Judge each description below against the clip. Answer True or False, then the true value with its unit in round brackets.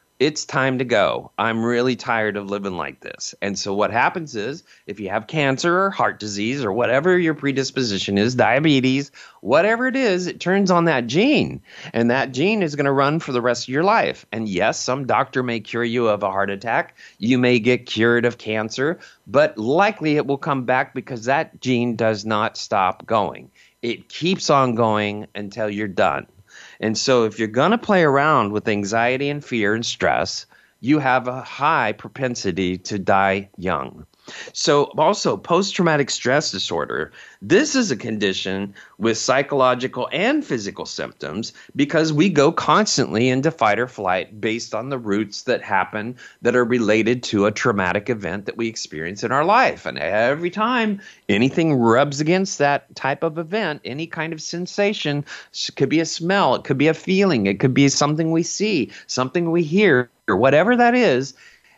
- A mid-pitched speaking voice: False (130 Hz)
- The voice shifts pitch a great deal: True (6.6 semitones)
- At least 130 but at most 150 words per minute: False (185 wpm)